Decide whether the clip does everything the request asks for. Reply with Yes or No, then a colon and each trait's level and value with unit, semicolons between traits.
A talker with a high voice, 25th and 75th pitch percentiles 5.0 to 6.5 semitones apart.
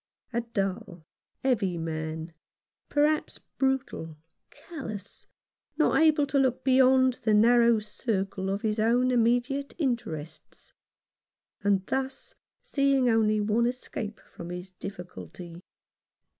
Yes: high, 225 Hz; average, 5.3 semitones